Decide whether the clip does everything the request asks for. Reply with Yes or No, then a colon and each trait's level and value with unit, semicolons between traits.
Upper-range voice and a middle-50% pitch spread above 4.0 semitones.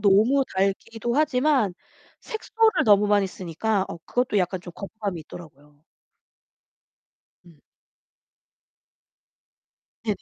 Yes: high, 205 Hz; average, 5.3 semitones